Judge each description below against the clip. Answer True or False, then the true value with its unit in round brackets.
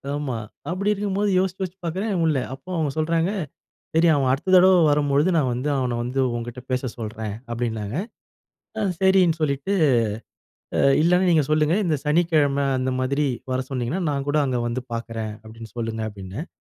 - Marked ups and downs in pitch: True (5.8 semitones)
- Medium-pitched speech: True (145 Hz)